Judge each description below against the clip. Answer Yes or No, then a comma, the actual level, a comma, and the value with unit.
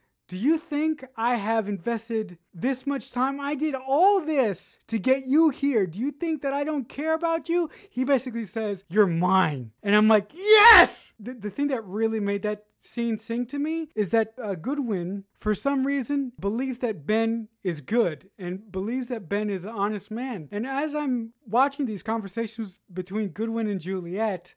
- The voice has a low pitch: No, high, 230 Hz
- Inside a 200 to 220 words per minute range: No, average, 185 wpm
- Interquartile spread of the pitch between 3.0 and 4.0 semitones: No, average, 5.0 semitones